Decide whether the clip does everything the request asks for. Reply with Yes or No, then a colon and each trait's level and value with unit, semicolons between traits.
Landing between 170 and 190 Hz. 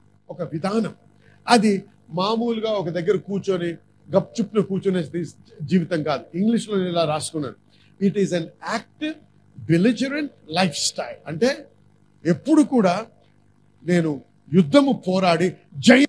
Yes: medium, 185 Hz